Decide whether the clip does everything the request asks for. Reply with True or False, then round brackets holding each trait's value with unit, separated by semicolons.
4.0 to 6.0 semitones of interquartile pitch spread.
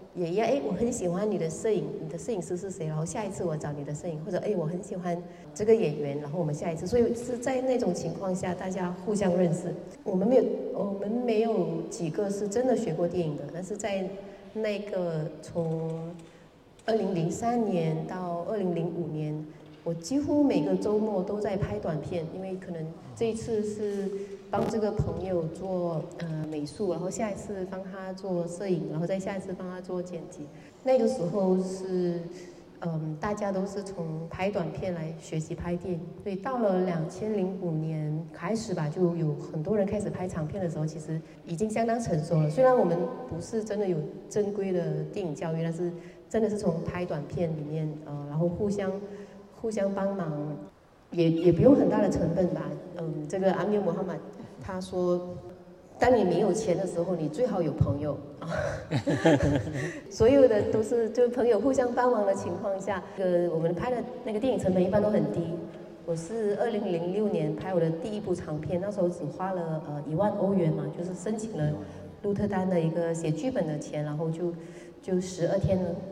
False (3.5 semitones)